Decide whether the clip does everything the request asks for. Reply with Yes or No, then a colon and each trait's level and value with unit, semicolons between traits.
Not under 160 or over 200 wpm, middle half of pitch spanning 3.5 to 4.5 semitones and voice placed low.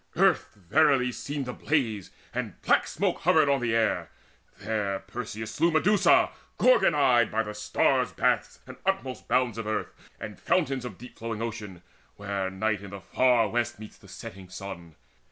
Yes: average, 165 wpm; average, 4.2 semitones; low, 115 Hz